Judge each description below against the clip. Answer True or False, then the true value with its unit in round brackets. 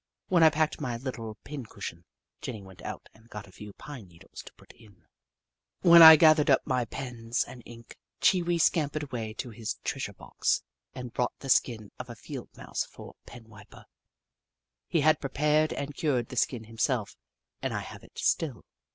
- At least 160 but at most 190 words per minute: True (185 wpm)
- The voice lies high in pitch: False (125 Hz)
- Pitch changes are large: False (5.0 semitones)